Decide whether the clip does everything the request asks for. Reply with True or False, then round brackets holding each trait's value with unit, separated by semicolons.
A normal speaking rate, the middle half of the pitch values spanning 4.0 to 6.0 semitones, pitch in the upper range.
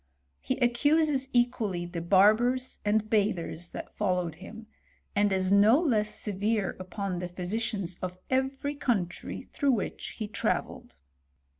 False (130 wpm; 4.6 semitones; 210 Hz)